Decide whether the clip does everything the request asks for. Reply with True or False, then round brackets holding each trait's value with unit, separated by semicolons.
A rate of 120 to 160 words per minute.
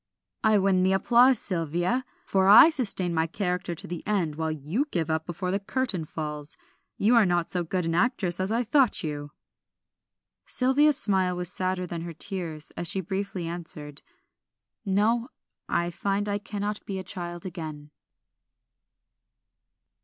True (155 wpm)